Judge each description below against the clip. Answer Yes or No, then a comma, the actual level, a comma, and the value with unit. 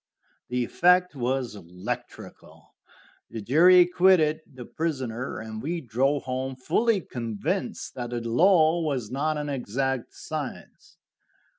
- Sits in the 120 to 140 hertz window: Yes, low, 135 Hz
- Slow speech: Yes, slow, 120 wpm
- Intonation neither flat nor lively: Yes, average, 5.0 semitones